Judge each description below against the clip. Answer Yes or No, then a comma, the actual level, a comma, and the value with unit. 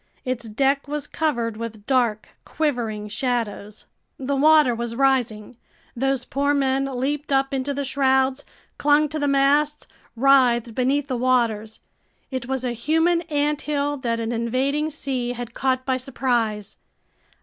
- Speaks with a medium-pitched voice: No, very high, 260 Hz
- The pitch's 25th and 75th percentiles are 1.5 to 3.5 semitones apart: Yes, average, 3.0 semitones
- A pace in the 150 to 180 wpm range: No, average, 140 wpm